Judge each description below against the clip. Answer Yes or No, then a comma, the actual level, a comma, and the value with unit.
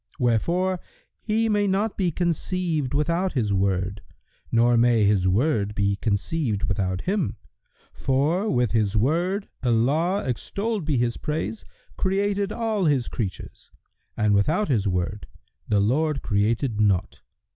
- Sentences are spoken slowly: Yes, slow, 130 wpm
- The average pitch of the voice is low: Yes, low, 130 Hz